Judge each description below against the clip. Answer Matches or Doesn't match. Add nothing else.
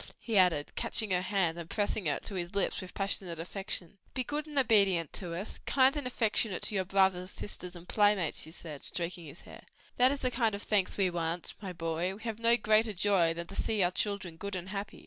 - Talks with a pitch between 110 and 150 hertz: Doesn't match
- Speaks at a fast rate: Matches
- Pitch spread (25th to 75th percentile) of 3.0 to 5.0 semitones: Matches